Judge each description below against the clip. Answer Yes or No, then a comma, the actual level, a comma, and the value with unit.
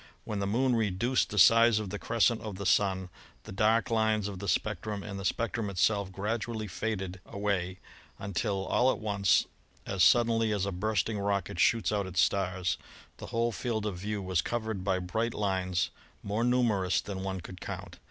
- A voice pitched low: Yes, low, 100 Hz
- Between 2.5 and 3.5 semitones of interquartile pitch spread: Yes, average, 2.8 semitones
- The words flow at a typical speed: Yes, average, 185 wpm